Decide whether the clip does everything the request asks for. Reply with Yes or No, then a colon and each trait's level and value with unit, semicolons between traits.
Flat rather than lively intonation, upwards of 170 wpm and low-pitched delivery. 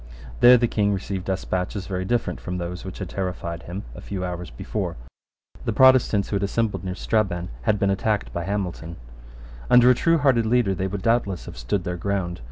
No: average, 3.5 semitones; average, 190 wpm; very low, 95 Hz